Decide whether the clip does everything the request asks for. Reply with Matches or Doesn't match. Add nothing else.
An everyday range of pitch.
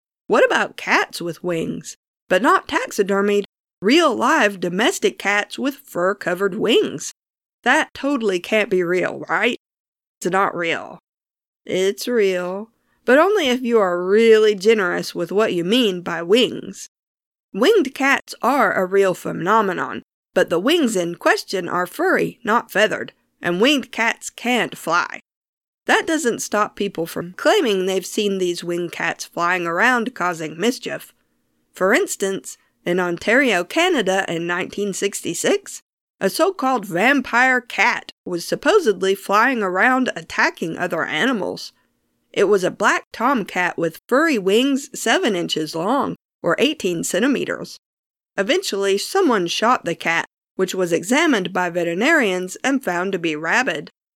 Doesn't match